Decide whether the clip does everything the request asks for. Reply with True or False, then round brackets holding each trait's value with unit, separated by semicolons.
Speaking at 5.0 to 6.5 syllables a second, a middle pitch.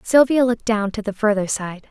False (5.5 syllables/s; 220 Hz)